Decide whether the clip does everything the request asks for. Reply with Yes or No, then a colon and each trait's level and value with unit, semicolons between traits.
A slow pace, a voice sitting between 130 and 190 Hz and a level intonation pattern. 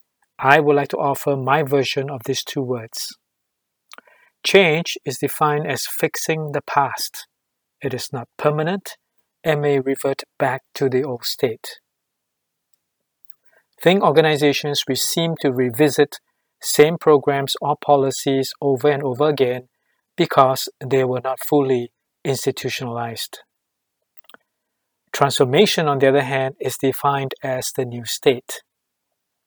Yes: slow, 125 wpm; medium, 140 Hz; narrow, 2.1 semitones